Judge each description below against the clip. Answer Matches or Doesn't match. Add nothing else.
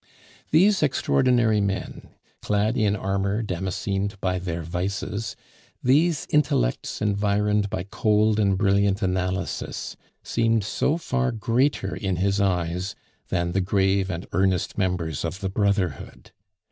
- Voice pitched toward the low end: Matches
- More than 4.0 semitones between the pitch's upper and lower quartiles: Doesn't match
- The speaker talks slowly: Matches